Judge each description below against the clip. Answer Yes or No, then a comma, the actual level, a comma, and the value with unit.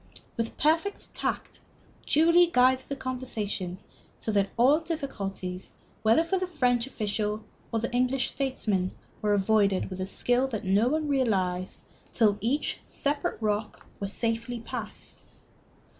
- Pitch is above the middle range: Yes, high, 230 Hz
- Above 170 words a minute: No, slow, 135 wpm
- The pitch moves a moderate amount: Yes, average, 4.9 semitones